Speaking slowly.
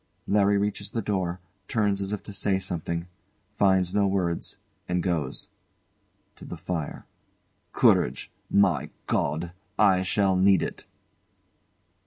Yes: slow, 125 wpm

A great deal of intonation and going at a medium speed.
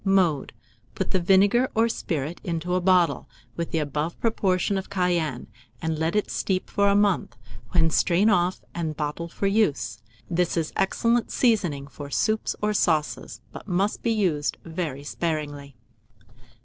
No: average, 4.2 semitones; average, 155 wpm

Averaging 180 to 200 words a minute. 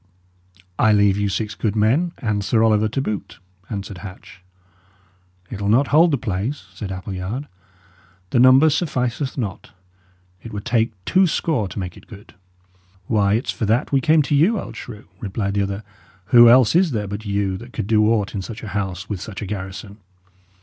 Yes: average, 185 wpm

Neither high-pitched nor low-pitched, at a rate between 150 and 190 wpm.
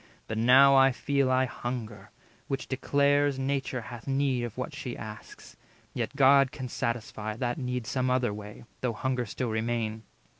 No: low, 125 Hz; average, 160 wpm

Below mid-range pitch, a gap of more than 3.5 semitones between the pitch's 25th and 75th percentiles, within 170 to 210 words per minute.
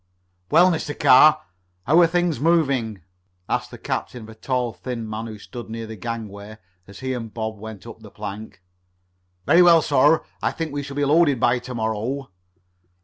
Yes: low, 125 Hz; average, 5.0 semitones; average, 185 wpm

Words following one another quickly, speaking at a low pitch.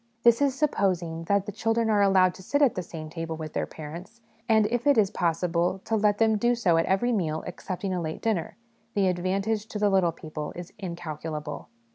No: fast, 210 wpm; high, 190 Hz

